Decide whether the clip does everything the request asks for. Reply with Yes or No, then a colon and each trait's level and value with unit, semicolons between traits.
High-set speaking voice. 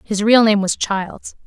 Yes: high, 205 Hz